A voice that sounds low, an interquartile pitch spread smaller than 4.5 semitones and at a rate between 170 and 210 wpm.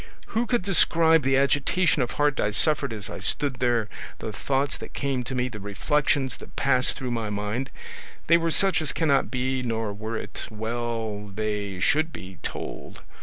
No: low, 125 Hz; average, 5.1 semitones; average, 180 wpm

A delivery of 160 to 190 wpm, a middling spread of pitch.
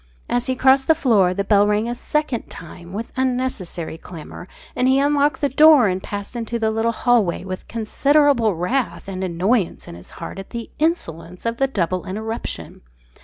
No: average, 180 wpm; wide, 5.8 semitones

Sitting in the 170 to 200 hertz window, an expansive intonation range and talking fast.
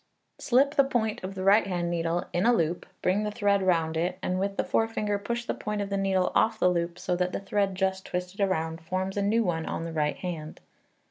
No: high, 190 Hz; average, 2.8 semitones; fast, 240 wpm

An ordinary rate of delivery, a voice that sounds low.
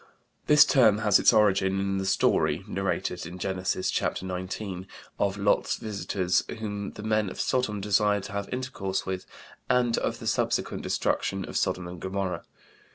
Yes: average, 160 wpm; low, 100 Hz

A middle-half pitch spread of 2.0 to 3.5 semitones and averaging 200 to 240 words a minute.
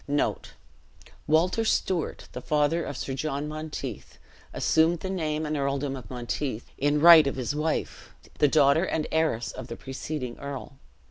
No: average, 2.7 semitones; average, 150 wpm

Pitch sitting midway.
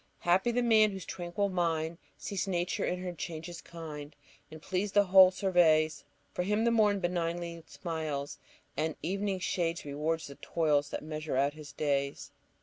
Yes: medium, 170 Hz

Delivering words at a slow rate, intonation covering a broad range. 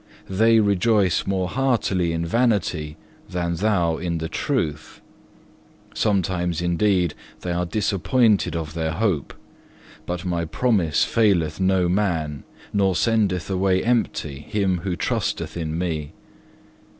No: slow, 120 wpm; average, 3.6 semitones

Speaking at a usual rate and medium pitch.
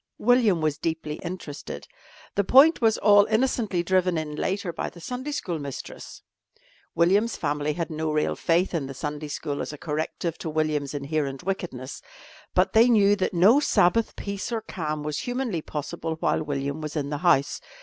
Yes: average, 175 wpm; medium, 165 Hz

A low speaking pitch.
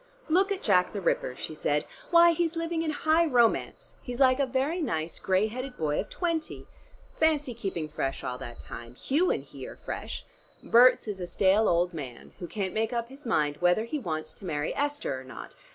No: high, 225 Hz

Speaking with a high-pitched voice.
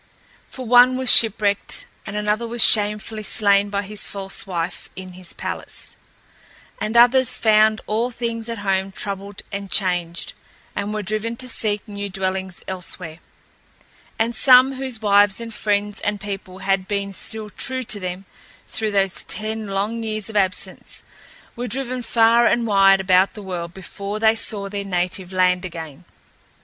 Yes: high, 205 Hz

